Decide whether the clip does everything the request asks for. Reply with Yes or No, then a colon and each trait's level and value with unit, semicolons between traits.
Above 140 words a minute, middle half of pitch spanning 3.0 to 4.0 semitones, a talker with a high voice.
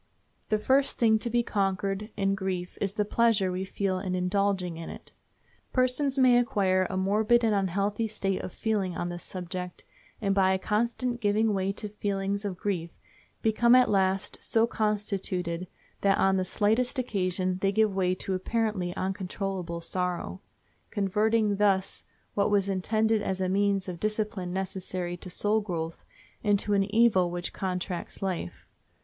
No: average, 155 wpm; narrow, 2.5 semitones; high, 195 Hz